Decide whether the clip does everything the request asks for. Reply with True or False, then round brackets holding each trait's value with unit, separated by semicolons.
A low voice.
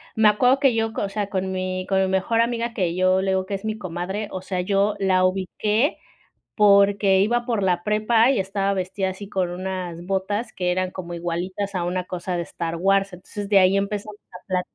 False (190 Hz)